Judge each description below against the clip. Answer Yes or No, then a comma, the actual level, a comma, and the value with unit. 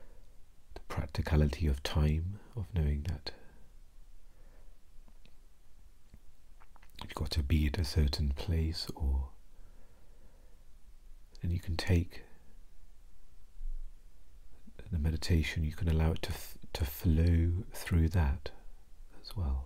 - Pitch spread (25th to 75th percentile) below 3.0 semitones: Yes, narrow, 2.6 semitones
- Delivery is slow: Yes, slow, 100 wpm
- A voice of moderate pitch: No, very low, 80 Hz